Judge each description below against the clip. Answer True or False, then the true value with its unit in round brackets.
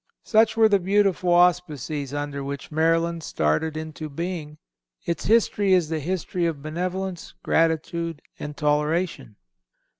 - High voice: False (165 Hz)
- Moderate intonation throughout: True (3.3 semitones)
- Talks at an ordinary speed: False (125 wpm)